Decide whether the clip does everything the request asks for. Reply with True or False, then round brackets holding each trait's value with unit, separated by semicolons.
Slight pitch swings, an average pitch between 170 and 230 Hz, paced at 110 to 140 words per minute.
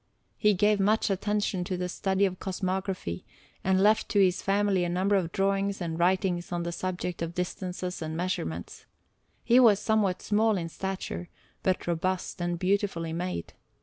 False (2.2 semitones; 185 Hz; 165 wpm)